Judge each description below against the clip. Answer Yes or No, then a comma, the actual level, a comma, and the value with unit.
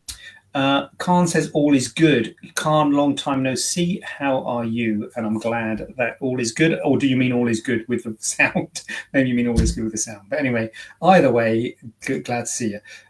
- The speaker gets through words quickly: Yes, fast, 225 wpm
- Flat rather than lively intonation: No, average, 3.6 semitones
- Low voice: Yes, low, 125 Hz